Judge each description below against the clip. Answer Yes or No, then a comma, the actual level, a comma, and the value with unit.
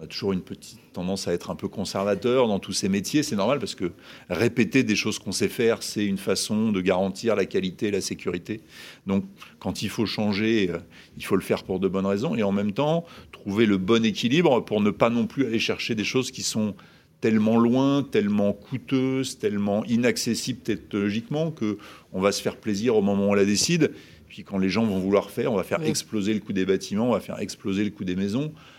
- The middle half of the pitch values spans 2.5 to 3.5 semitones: Yes, average, 3.1 semitones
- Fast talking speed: Yes, fast, 225 wpm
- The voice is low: Yes, low, 105 Hz